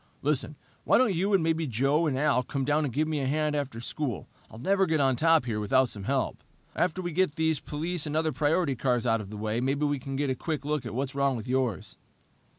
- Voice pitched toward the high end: No, medium, 140 Hz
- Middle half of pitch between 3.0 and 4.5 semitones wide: Yes, average, 3.7 semitones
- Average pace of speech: No, fast, 250 wpm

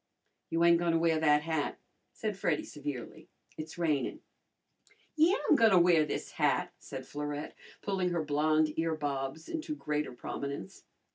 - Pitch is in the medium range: Yes, medium, 160 Hz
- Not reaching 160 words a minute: Yes, average, 140 wpm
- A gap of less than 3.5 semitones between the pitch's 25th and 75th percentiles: Yes, average, 2.8 semitones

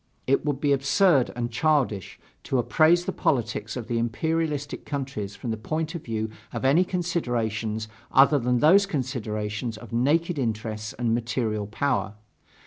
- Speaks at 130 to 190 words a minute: Yes, average, 150 wpm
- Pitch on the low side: Yes, low, 125 Hz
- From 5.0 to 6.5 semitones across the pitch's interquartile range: Yes, average, 5.3 semitones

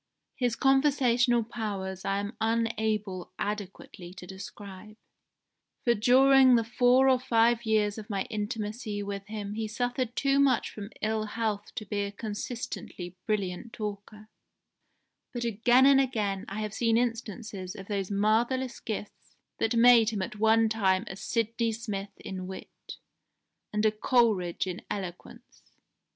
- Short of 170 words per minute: Yes, average, 140 wpm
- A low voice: No, high, 215 Hz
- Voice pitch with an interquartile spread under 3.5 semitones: Yes, average, 2.8 semitones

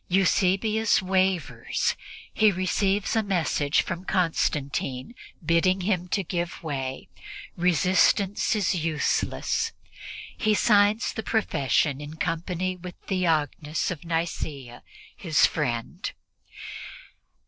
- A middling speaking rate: No, slow, 95 wpm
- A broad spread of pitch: No, average, 3.7 semitones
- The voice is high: No, medium, 180 Hz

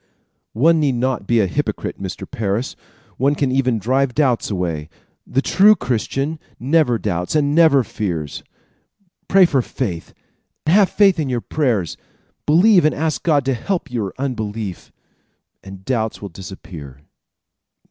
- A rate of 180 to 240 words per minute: No, average, 140 wpm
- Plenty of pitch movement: Yes, wide, 6.8 semitones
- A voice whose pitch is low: Yes, low, 125 Hz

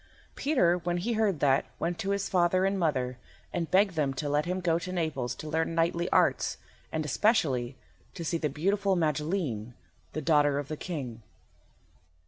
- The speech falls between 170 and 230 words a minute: Yes, average, 175 wpm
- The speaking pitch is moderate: Yes, medium, 165 Hz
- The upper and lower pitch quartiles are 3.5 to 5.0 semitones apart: Yes, average, 4.1 semitones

